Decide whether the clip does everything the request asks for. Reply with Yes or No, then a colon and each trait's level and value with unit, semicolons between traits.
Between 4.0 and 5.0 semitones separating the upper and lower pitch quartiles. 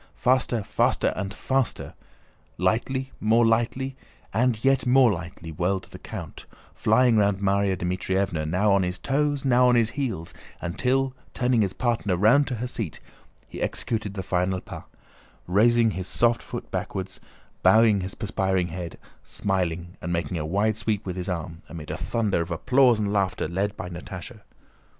Yes: average, 4.7 semitones